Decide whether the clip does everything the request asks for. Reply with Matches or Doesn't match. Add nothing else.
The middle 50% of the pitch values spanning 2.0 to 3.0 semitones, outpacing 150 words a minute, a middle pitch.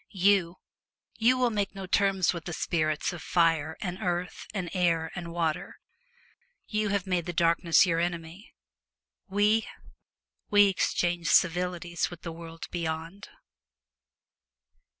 Doesn't match